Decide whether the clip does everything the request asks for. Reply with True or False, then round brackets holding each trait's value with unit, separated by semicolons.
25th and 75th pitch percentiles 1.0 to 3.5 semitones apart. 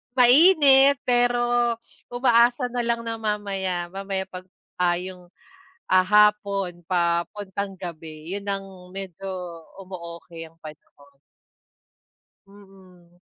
False (4.1 semitones)